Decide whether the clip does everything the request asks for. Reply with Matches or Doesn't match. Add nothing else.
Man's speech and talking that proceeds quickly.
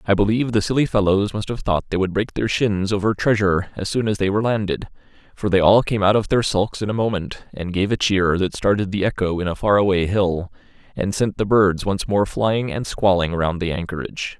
Matches